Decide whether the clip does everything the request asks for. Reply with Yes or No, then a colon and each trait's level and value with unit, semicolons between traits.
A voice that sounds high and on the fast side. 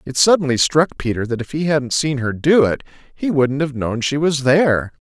No: medium, 140 Hz; fast, 225 wpm